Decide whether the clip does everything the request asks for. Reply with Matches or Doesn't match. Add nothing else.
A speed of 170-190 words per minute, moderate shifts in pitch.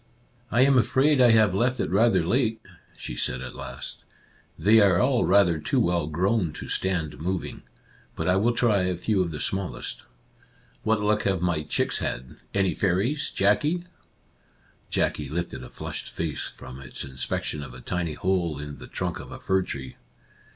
Doesn't match